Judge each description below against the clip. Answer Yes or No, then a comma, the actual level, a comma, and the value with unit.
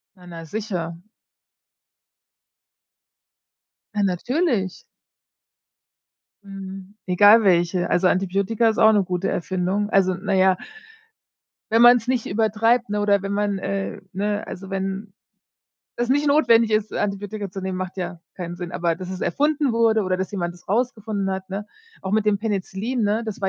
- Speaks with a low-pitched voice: No, high, 200 Hz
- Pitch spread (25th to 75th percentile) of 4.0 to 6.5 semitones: No, average, 2.7 semitones